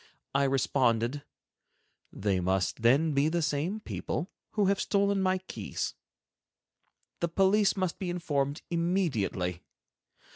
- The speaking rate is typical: No, slow, 115 wpm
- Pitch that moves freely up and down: Yes, wide, 6.5 semitones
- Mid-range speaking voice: Yes, medium, 160 Hz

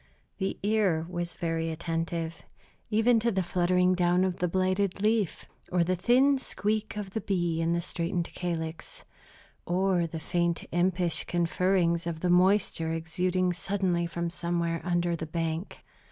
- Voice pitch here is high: No, medium, 175 Hz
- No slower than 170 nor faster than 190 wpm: No, average, 150 wpm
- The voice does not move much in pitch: Yes, narrow, 2.0 semitones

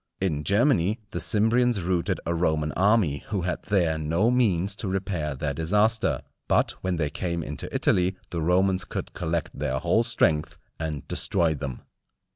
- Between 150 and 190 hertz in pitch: No, very low, 90 Hz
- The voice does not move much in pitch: No, average, 4.2 semitones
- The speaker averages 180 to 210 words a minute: No, average, 160 wpm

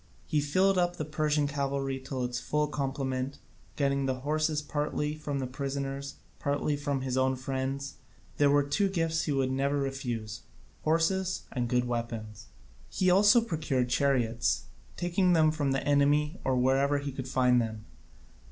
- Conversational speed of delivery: Yes, average, 160 wpm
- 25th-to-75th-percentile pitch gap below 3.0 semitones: Yes, narrow, 2.4 semitones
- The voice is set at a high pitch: No, medium, 140 Hz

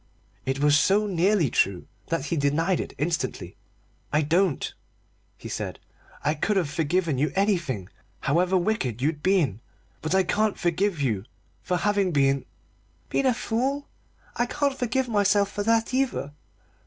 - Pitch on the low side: No, medium, 180 Hz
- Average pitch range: No, wide, 6.1 semitones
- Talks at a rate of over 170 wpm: No, average, 155 wpm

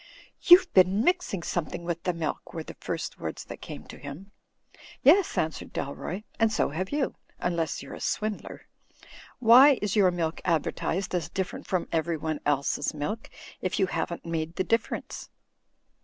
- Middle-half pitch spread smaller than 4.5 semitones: No, average, 4.9 semitones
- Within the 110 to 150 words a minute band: No, average, 160 wpm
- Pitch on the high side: No, medium, 180 Hz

